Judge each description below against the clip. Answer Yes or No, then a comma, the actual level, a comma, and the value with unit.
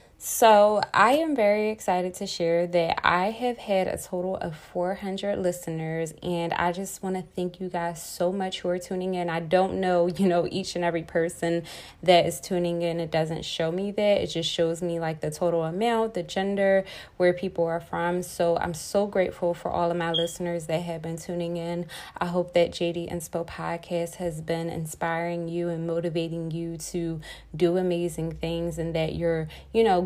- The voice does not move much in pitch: Yes, narrow, 1.6 semitones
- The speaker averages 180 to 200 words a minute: Yes, average, 195 wpm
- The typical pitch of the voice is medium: Yes, medium, 175 Hz